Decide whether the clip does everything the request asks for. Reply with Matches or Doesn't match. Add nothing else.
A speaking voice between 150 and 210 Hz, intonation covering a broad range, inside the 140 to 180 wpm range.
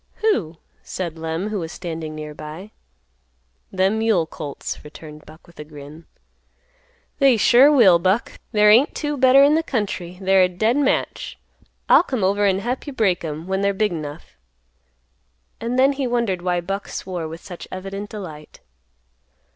Matches